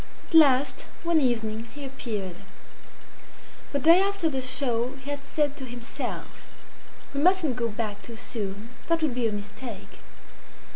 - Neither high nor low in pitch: No, very high, 255 Hz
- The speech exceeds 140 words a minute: Yes, average, 150 wpm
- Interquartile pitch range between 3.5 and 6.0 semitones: Yes, average, 4.2 semitones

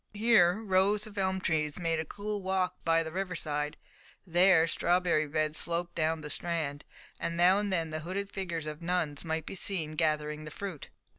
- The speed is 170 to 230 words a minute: Yes, average, 190 wpm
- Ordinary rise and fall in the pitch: Yes, average, 3.3 semitones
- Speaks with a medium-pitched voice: Yes, medium, 170 Hz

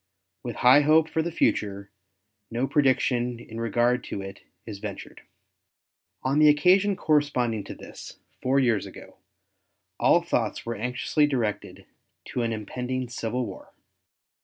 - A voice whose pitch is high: No, low, 125 Hz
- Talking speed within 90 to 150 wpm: Yes, slow, 135 wpm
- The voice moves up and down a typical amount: Yes, average, 4.3 semitones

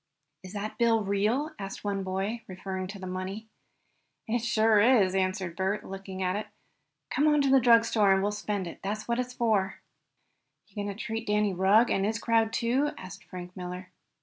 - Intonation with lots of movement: No, average, 3.1 semitones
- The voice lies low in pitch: No, high, 205 Hz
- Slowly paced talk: No, average, 185 wpm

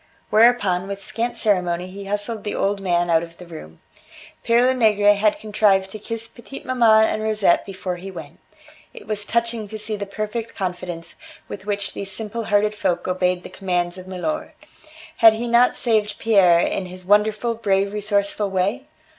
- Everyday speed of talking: Yes, average, 175 wpm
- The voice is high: Yes, high, 205 Hz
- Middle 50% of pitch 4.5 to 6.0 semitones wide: No, average, 2.9 semitones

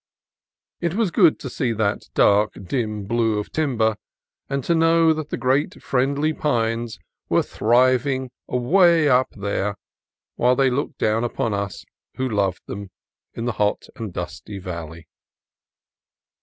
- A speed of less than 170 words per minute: Yes, average, 140 wpm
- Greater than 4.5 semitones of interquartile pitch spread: Yes, average, 5.2 semitones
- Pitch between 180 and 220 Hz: No, low, 120 Hz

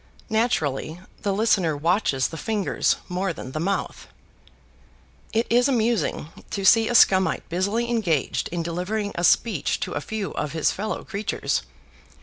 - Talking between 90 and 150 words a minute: Yes, average, 145 wpm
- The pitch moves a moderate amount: Yes, average, 5.0 semitones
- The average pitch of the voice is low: No, high, 195 Hz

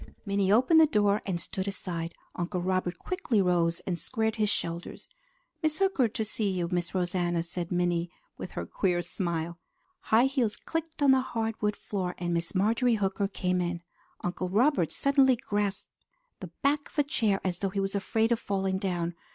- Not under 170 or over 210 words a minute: Yes, average, 180 wpm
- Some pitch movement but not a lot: Yes, average, 4.2 semitones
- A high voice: Yes, high, 195 Hz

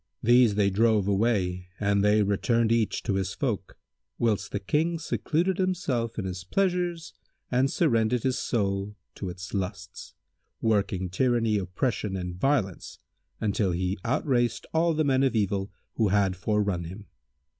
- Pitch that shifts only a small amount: No, average, 4.5 semitones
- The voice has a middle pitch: No, low, 105 Hz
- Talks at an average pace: Yes, average, 145 wpm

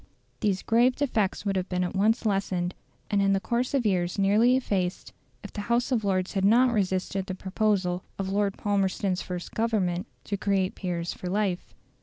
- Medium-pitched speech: No, high, 195 Hz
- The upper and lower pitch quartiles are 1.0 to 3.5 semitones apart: Yes, average, 2.7 semitones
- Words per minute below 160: No, average, 185 wpm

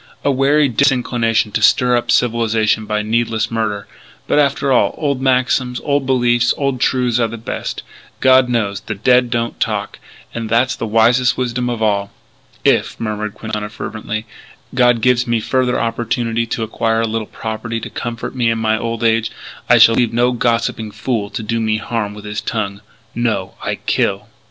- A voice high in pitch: No, low, 115 Hz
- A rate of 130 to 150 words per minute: No, average, 175 wpm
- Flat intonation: Yes, narrow, 2.1 semitones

